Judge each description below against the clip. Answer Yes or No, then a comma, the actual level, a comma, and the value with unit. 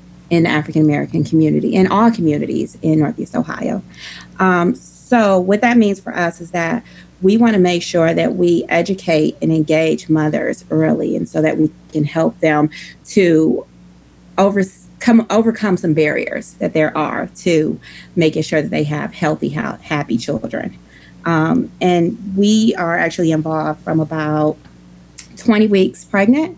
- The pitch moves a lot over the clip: No, average, 3.8 semitones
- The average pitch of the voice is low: No, medium, 165 Hz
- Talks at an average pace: Yes, average, 150 wpm